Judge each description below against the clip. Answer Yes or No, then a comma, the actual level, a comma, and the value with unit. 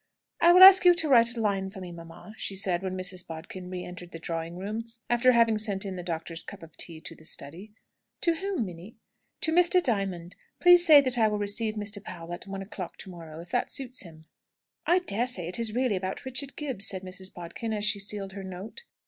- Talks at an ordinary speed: No, fast, 225 wpm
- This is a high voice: Yes, high, 200 Hz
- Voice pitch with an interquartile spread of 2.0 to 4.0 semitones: No, average, 4.8 semitones